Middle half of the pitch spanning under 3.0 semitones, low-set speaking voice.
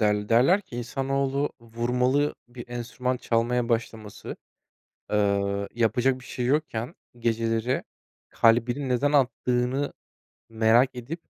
Yes: narrow, 2.5 semitones; low, 120 Hz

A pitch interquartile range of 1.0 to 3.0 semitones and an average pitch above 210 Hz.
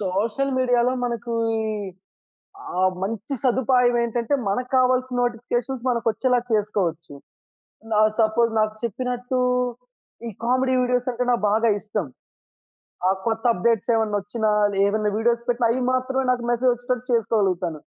Yes: narrow, 2.6 semitones; high, 235 Hz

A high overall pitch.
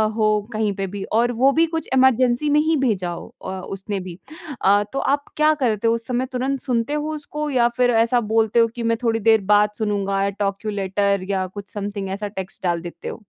Yes: high, 220 Hz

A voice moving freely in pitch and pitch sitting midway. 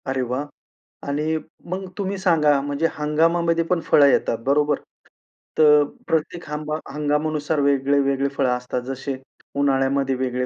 No: narrow, 2.4 semitones; medium, 145 Hz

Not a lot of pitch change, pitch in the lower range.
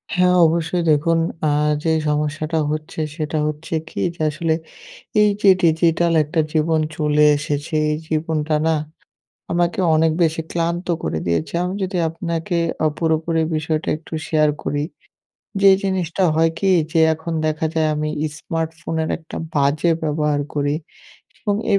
No: narrow, 1.7 semitones; medium, 160 Hz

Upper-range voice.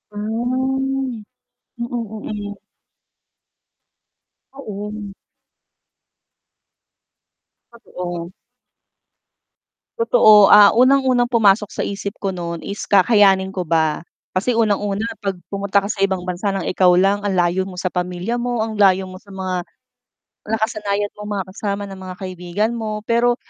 Yes: high, 205 Hz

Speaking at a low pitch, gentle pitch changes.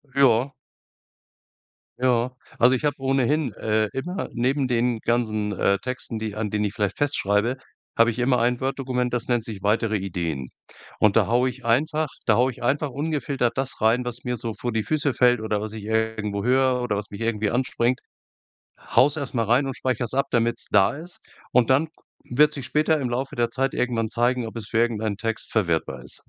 No: low, 120 Hz; average, 3.1 semitones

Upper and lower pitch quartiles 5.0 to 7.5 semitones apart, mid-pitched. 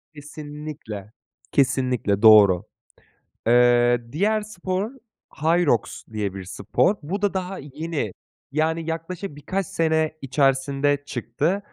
Yes: wide, 5.4 semitones; medium, 145 Hz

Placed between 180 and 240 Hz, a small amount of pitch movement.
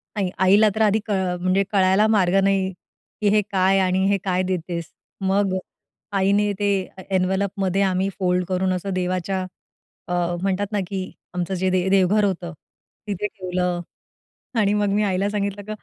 Yes: high, 190 Hz; narrow, 1.6 semitones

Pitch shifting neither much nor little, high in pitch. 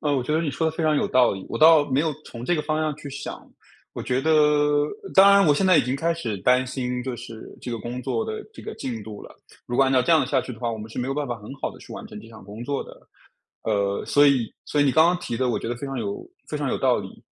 No: average, 4.2 semitones; low, 135 Hz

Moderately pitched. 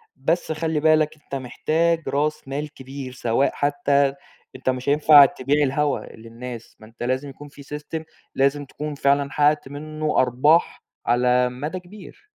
Yes: medium, 145 Hz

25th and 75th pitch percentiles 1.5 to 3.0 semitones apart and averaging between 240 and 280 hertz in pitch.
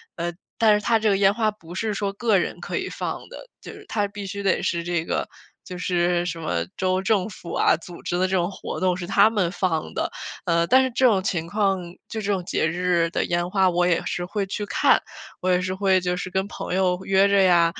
No: narrow, 2.5 semitones; medium, 185 Hz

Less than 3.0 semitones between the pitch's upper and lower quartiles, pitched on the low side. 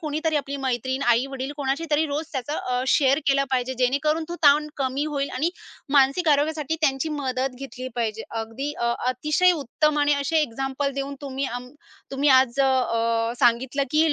No: narrow, 2.6 semitones; very high, 275 Hz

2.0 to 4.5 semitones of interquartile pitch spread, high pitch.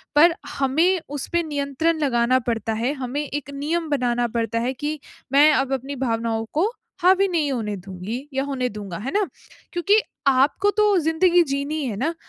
No: average, 4.9 semitones; very high, 275 Hz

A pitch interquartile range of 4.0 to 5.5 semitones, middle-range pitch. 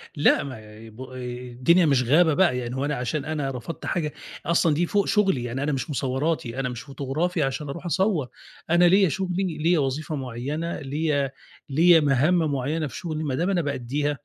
Yes: average, 4.3 semitones; medium, 145 Hz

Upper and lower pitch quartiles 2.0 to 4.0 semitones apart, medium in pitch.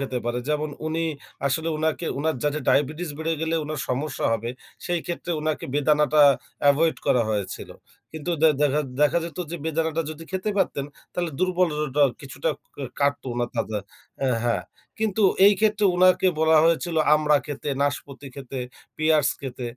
Yes: average, 2.7 semitones; medium, 155 Hz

